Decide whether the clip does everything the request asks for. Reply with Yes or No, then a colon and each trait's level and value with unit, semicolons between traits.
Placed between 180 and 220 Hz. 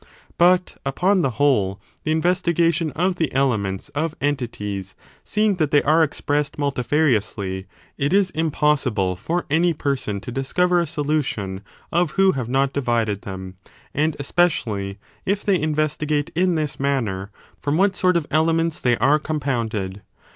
No: medium, 145 Hz